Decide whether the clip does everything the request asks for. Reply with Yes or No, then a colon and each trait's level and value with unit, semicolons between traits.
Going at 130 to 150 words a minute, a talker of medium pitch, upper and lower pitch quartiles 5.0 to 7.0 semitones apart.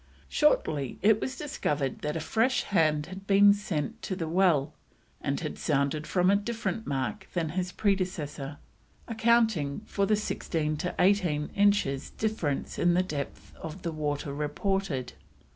Yes: average, 145 wpm; medium, 180 Hz; wide, 5.4 semitones